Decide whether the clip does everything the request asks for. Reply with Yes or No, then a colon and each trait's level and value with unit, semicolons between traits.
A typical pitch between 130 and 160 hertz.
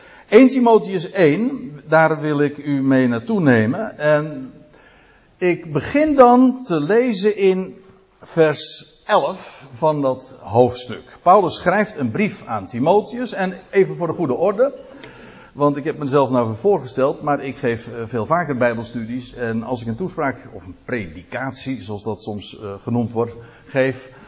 Yes: medium, 140 Hz